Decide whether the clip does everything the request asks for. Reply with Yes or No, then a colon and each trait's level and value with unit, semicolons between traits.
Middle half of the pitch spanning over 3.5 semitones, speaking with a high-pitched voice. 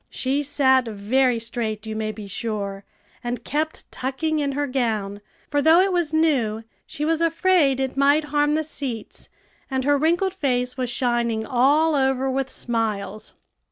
Yes: average, 4.6 semitones; very high, 265 Hz